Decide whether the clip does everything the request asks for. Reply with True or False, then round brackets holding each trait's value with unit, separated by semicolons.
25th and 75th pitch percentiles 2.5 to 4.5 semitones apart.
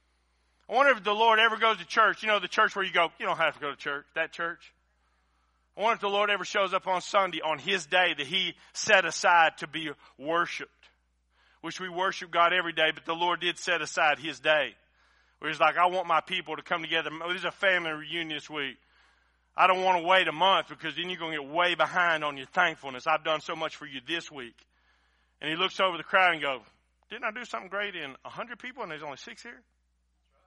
True (3.8 semitones)